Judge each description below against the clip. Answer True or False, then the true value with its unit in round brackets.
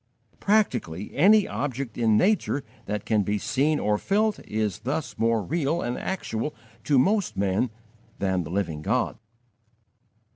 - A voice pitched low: True (120 Hz)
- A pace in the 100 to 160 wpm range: True (140 wpm)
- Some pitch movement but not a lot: False (7.5 semitones)